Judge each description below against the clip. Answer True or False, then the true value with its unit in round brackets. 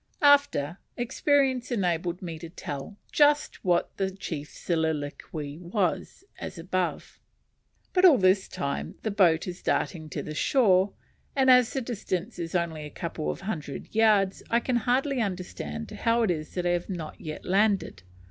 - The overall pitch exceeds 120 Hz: True (185 Hz)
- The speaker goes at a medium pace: True (160 wpm)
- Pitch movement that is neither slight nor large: False (5.9 semitones)